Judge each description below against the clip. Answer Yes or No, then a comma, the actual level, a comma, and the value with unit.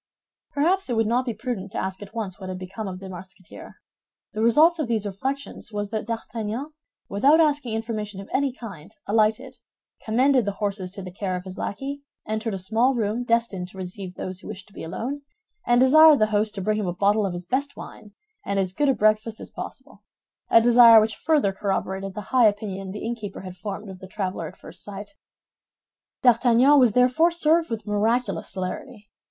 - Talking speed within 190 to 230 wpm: Yes, average, 200 wpm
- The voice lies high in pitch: Yes, high, 215 Hz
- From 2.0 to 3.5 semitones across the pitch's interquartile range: No, average, 4.2 semitones